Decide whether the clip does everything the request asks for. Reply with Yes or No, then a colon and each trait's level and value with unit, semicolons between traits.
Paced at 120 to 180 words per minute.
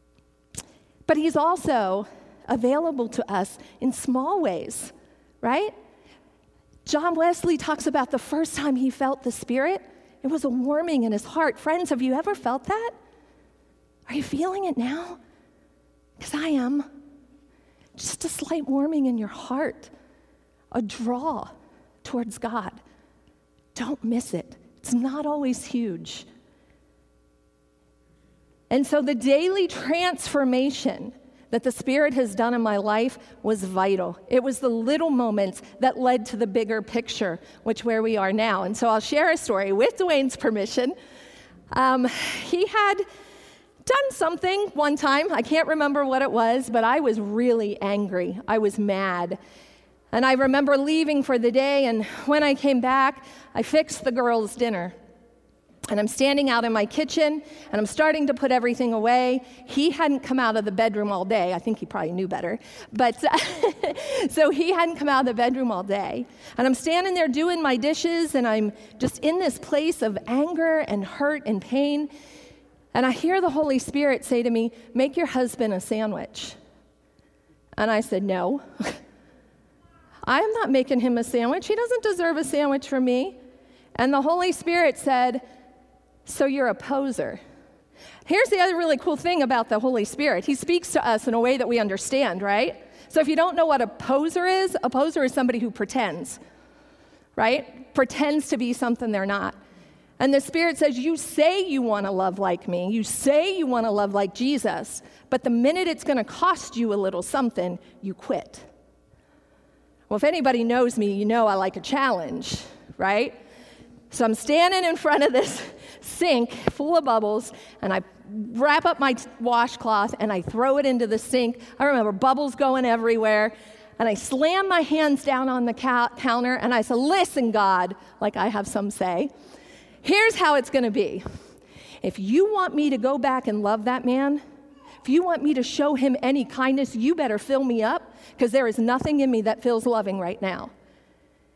Yes: average, 175 wpm